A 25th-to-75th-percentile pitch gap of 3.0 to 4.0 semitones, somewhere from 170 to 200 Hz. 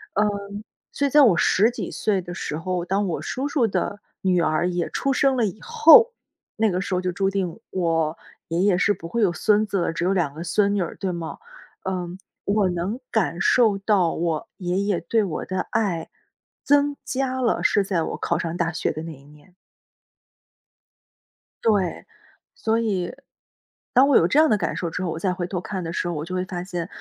Yes: average, 3.7 semitones; medium, 185 Hz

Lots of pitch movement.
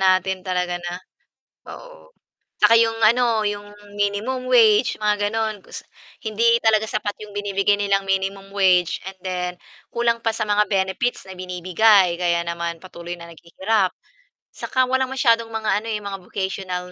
No: average, 3.1 semitones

